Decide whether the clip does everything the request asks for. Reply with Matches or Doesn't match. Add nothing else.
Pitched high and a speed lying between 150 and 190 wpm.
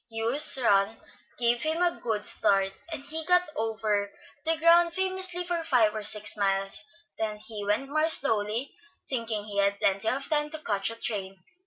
Matches